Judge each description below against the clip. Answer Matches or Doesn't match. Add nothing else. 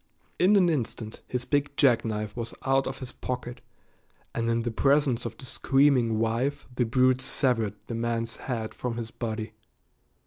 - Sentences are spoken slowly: Doesn't match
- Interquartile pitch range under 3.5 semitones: Matches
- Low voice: Matches